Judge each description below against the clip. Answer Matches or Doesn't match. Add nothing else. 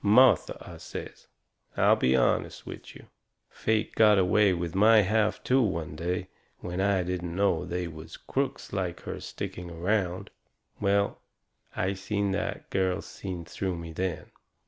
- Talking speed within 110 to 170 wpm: Matches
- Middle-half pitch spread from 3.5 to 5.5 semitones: Doesn't match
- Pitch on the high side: Doesn't match